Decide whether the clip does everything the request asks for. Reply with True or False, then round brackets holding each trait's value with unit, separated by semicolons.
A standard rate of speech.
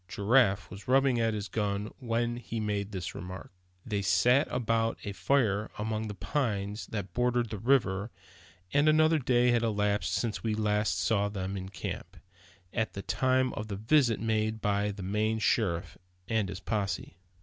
True (170 wpm)